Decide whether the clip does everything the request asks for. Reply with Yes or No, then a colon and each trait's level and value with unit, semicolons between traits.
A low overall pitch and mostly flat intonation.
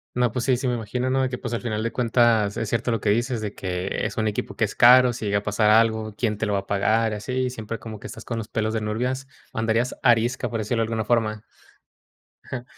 Yes: low, 115 Hz; narrow, 2.3 semitones